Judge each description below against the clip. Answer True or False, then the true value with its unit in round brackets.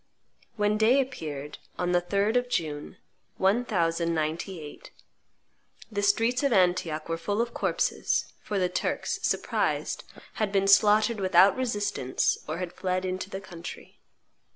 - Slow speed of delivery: True (130 wpm)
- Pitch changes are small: False (3.9 semitones)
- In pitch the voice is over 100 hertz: True (190 Hz)